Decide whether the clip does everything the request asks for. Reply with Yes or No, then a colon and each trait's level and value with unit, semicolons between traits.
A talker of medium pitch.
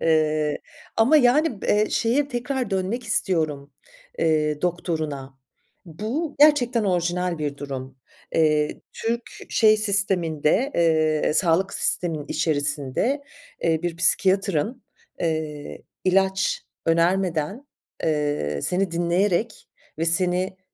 Yes: medium, 175 Hz